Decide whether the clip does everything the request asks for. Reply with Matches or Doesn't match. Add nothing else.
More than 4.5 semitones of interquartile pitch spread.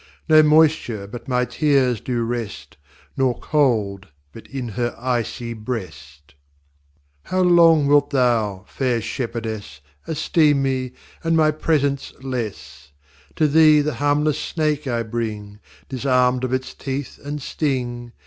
Doesn't match